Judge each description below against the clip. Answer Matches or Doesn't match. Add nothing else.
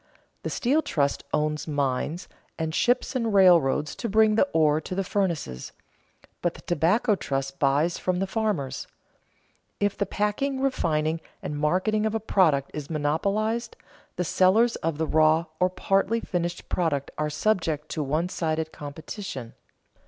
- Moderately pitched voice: Matches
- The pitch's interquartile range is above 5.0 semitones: Matches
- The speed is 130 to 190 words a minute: Matches